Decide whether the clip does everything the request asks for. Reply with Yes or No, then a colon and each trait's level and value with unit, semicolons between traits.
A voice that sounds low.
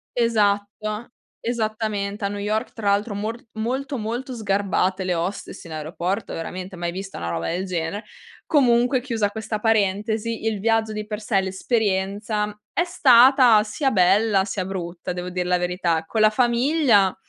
No: high, 210 Hz